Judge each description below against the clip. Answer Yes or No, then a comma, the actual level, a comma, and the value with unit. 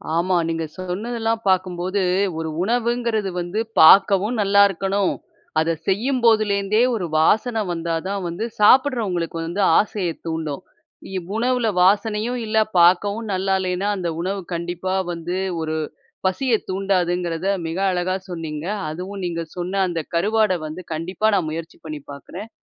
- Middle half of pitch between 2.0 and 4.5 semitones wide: Yes, average, 3.7 semitones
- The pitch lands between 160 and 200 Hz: Yes, high, 190 Hz